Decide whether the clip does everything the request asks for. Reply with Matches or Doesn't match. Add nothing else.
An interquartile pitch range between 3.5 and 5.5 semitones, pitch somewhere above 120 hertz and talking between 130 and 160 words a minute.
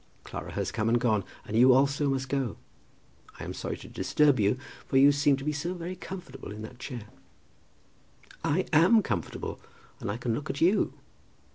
Doesn't match